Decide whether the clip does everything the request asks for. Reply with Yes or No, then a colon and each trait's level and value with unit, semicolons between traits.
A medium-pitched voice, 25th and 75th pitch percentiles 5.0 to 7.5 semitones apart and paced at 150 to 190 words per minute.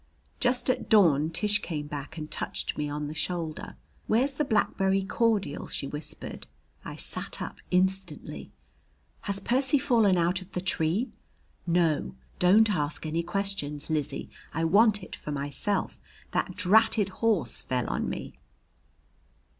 No: medium, 180 Hz; wide, 5.5 semitones; average, 140 wpm